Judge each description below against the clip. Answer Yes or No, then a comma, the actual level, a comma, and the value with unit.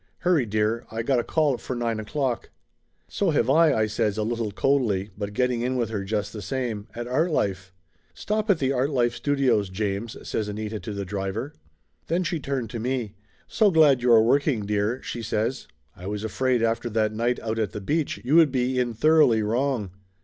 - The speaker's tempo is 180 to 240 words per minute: Yes, average, 200 wpm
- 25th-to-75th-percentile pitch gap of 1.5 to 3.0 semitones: No, average, 3.8 semitones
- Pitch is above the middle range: No, low, 120 Hz